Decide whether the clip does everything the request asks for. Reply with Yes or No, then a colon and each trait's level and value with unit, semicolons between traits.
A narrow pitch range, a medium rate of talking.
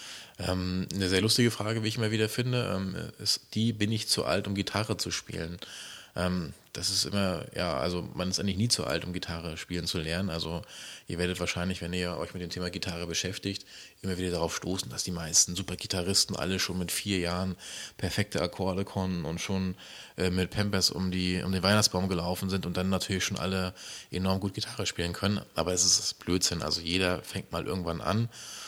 No: narrow, 1.9 semitones; fast, 200 wpm